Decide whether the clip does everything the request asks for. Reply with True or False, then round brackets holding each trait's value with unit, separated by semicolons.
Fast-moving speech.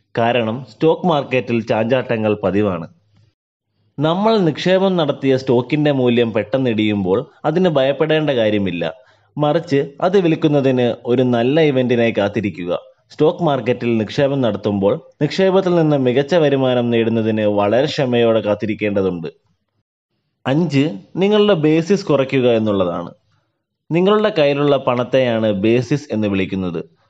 False (100 wpm)